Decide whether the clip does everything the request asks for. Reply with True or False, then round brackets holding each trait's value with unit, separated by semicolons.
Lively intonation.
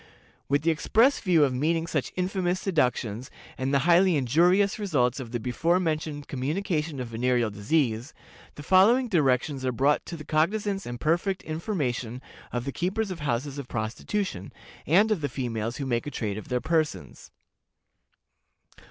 True (6.1 semitones)